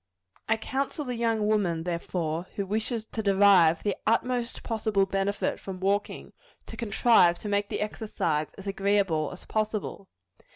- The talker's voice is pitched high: Yes, high, 200 Hz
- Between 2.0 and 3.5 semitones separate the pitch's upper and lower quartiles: Yes, average, 2.9 semitones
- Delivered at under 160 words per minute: Yes, average, 150 wpm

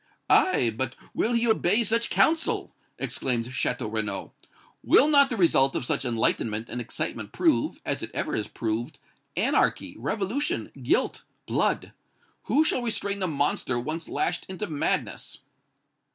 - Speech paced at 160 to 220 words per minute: No, average, 140 wpm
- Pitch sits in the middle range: Yes, medium, 160 Hz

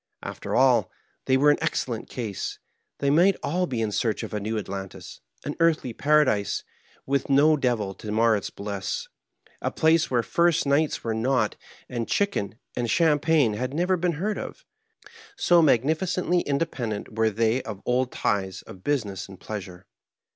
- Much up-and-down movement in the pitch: Yes, wide, 6.6 semitones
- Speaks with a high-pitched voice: No, low, 125 Hz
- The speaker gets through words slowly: No, average, 165 wpm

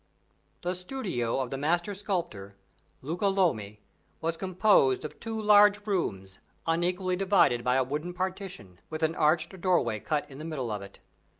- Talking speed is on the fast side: No, average, 160 wpm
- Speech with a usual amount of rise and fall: No, wide, 6.6 semitones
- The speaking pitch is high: No, medium, 165 Hz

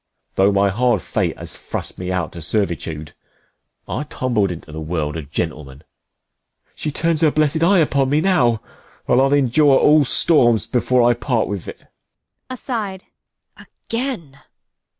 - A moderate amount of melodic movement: No, wide, 8.8 semitones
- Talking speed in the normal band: Yes, average, 150 wpm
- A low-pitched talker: Yes, low, 125 Hz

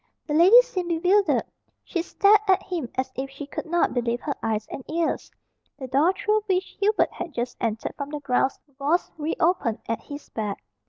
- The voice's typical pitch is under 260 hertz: No, very high, 305 Hz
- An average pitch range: No, wide, 5.8 semitones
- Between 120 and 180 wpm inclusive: No, average, 195 wpm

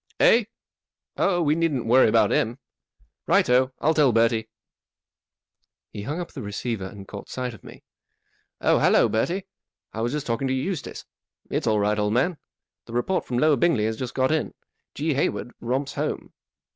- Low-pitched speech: Yes, low, 125 Hz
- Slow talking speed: No, average, 185 wpm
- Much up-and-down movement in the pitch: No, average, 5.0 semitones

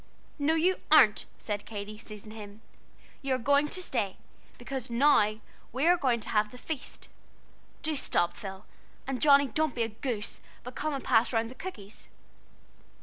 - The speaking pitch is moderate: No, high, 245 Hz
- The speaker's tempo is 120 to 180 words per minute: Yes, average, 170 wpm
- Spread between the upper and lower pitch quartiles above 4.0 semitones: Yes, average, 5.0 semitones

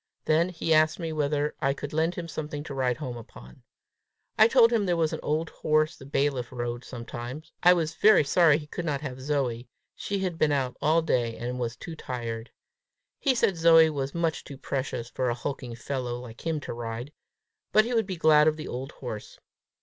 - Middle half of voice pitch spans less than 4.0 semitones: No, average, 4.6 semitones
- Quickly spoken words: Yes, fast, 210 wpm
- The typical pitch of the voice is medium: Yes, medium, 145 Hz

